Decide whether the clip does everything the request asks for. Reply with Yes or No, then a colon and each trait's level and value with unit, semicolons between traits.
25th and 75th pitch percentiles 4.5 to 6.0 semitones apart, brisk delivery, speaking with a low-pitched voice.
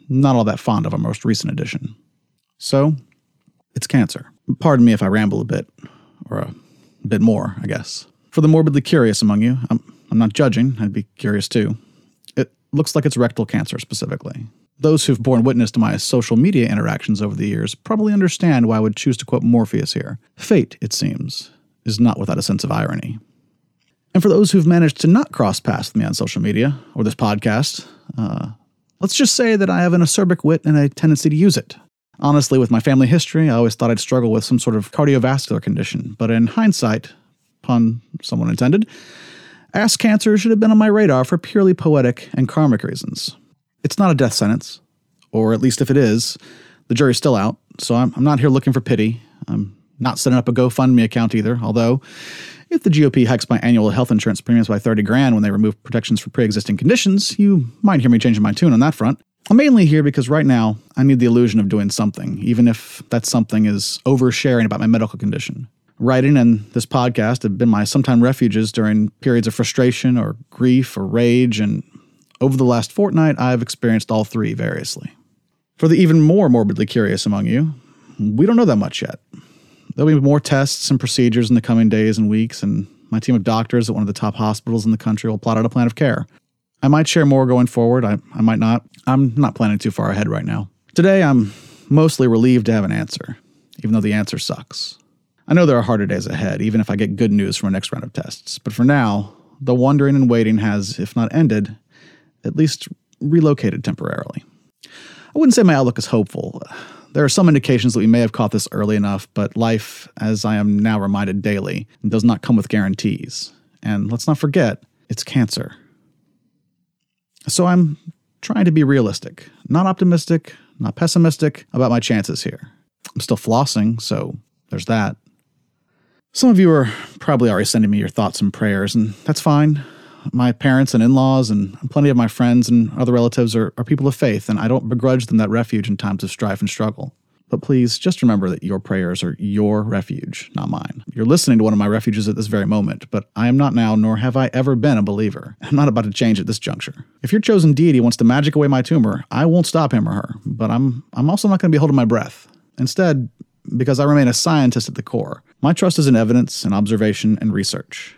Yes: average, 5.1 semitones; fast, 215 wpm; low, 125 Hz